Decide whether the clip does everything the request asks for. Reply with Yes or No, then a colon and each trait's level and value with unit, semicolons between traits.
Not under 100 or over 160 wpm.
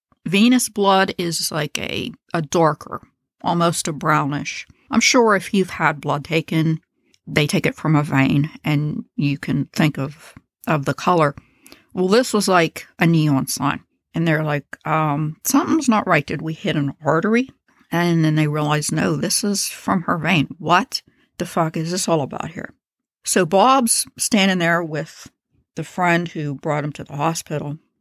No: average, 175 wpm